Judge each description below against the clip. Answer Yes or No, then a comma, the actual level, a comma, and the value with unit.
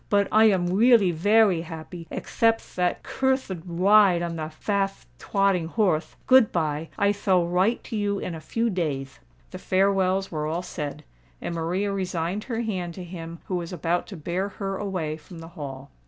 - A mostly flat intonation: No, average, 3.4 semitones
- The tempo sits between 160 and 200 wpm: Yes, average, 175 wpm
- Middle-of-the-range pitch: Yes, medium, 180 Hz